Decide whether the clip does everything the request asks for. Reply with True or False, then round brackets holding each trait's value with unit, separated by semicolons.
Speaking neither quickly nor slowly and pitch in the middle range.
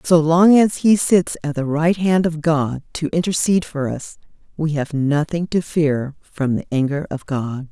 True (195 wpm; 155 Hz)